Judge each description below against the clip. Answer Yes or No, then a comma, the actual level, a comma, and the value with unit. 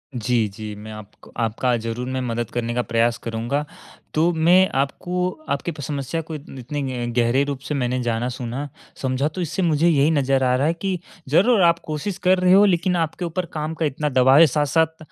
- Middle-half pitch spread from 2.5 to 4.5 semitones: No, average, 5.2 semitones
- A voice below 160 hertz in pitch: Yes, medium, 140 Hz